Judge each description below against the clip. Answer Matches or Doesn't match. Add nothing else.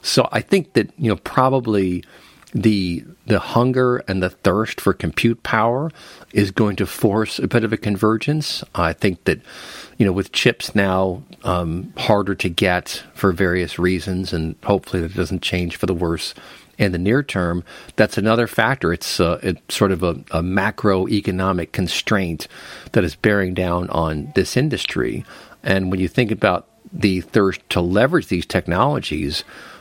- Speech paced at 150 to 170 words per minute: Matches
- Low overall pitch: Matches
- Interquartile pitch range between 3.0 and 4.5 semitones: Matches